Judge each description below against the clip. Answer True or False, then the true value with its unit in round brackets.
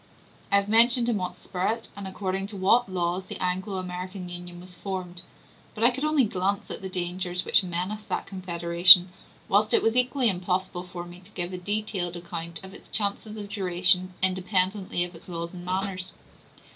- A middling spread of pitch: False (2.1 semitones)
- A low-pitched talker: False (185 Hz)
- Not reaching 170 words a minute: False (185 wpm)